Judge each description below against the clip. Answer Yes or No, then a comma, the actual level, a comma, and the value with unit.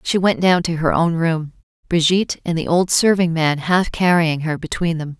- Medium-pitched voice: Yes, medium, 170 Hz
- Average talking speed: No, fast, 210 wpm